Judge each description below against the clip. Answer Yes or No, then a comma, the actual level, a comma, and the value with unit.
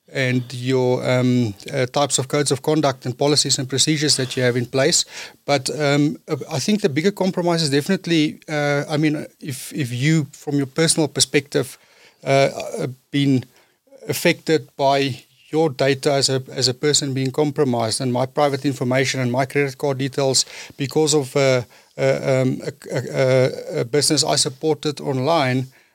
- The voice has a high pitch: No, medium, 140 Hz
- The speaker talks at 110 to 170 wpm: Yes, average, 165 wpm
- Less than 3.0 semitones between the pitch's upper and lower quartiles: Yes, narrow, 2.5 semitones